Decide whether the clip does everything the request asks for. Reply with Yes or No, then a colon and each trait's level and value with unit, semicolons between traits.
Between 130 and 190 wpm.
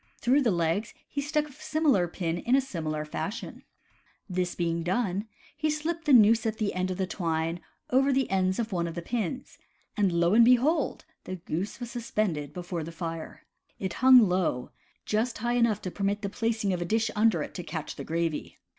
No: fast, 205 wpm